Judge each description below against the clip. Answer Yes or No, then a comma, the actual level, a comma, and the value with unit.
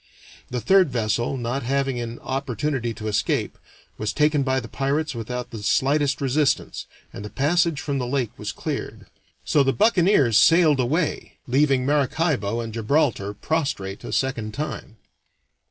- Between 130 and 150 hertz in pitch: Yes, low, 135 Hz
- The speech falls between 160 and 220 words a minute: No, average, 150 wpm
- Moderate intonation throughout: Yes, average, 4.1 semitones